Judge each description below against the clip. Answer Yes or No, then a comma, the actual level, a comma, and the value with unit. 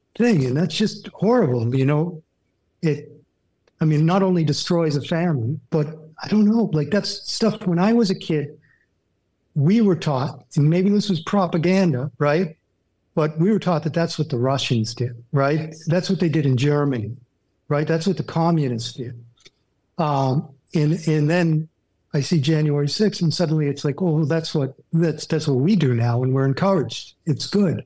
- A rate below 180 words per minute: No, average, 185 wpm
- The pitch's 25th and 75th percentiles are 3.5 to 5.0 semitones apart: Yes, average, 4.4 semitones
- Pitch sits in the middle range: Yes, medium, 155 Hz